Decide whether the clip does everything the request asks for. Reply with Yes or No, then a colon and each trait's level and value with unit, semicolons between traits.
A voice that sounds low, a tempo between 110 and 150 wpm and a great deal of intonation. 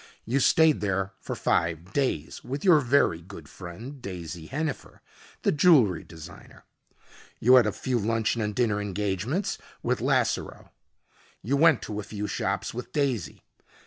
Yes: low, 110 Hz; average, 145 wpm; wide, 6.1 semitones